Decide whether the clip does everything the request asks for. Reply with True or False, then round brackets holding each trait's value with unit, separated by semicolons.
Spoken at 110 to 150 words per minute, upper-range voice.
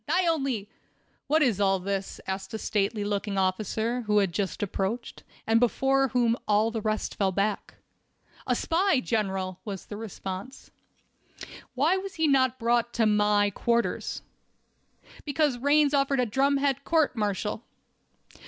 True (145 wpm; 225 Hz)